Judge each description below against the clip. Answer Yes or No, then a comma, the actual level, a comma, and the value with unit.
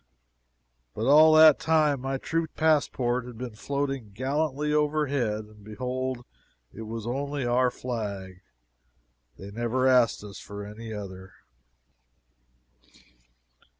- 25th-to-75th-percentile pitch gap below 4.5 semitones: No, average, 4.9 semitones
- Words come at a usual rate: No, slow, 115 wpm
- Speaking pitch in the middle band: No, low, 125 Hz